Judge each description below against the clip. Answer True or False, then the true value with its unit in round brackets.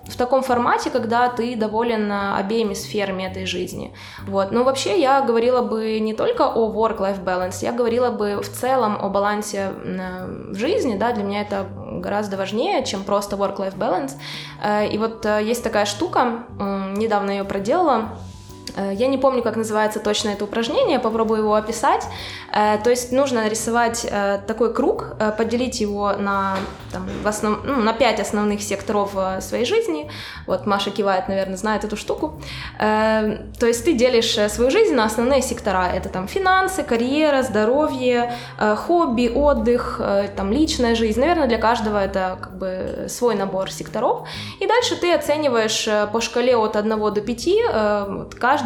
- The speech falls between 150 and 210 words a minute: True (155 wpm)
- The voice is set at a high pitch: True (220 Hz)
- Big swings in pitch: False (3.3 semitones)